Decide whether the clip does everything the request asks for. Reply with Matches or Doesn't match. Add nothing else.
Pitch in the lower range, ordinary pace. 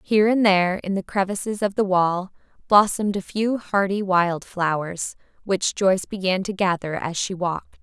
Doesn't match